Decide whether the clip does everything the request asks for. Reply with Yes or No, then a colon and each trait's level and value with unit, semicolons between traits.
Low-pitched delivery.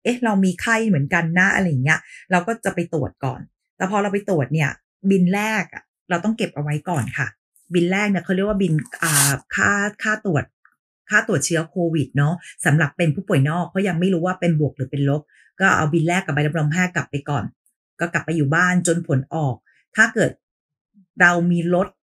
No: medium, 170 Hz